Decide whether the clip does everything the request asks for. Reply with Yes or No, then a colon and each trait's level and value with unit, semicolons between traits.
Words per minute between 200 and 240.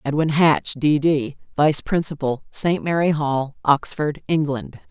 No: slow, 135 wpm